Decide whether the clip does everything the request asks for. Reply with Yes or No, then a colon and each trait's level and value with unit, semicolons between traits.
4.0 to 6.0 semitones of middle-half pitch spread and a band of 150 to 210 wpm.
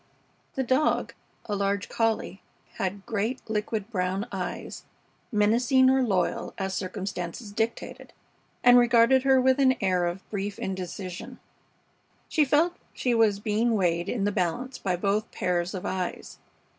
No: average, 4.5 semitones; average, 140 wpm